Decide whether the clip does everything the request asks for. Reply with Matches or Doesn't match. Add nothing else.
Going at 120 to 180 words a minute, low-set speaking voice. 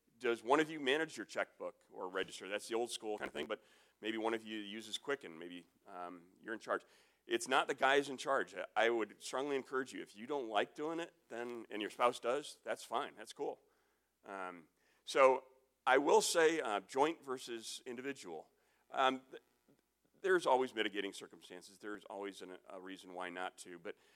Doesn't match